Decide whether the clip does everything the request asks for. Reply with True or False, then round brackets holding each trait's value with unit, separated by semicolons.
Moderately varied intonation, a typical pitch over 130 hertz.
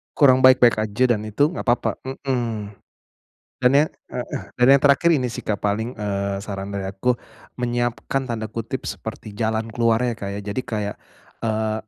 False (3.0 semitones; 115 Hz)